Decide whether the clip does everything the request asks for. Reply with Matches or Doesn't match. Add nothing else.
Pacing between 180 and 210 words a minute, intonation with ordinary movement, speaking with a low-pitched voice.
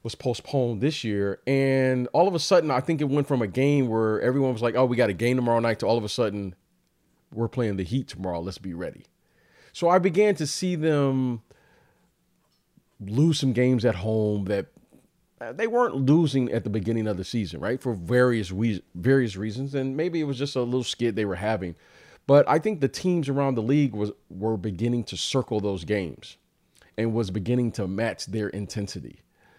Matches